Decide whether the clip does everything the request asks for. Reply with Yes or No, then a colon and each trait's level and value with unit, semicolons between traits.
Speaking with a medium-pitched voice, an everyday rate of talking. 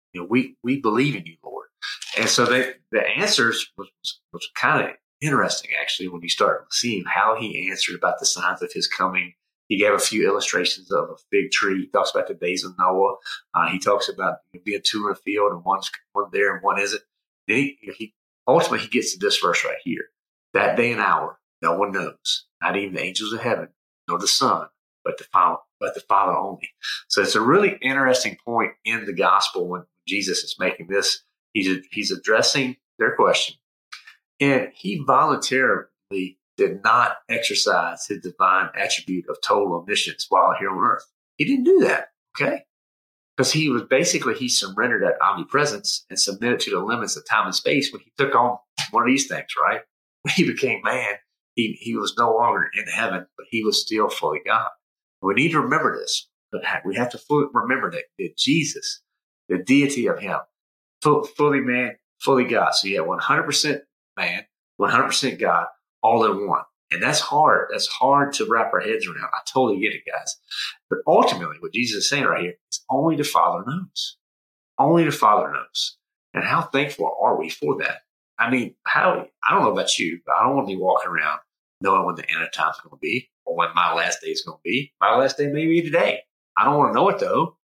No: medium, 180 Hz; fast, 210 wpm